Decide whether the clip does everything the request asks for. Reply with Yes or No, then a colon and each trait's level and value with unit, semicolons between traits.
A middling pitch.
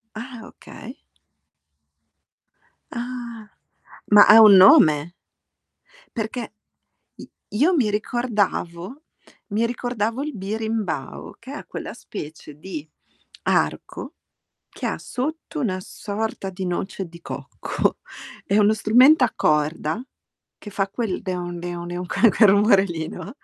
No: high, 210 Hz